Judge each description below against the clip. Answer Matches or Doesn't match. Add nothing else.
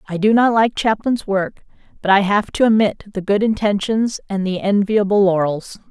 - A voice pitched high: Matches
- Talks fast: Doesn't match